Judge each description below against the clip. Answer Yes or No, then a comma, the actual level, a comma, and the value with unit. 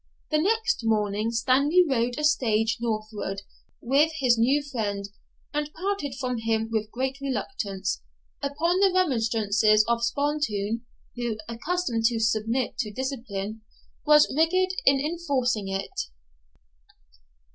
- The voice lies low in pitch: No, high, 245 Hz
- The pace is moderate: No, slow, 120 wpm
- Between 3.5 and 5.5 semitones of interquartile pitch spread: Yes, average, 5.2 semitones